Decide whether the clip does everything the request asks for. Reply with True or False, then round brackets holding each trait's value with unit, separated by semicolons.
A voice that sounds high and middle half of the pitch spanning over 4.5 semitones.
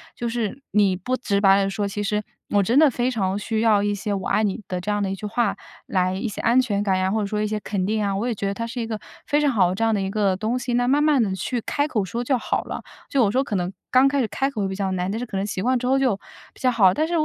False (215 Hz; 3.7 semitones)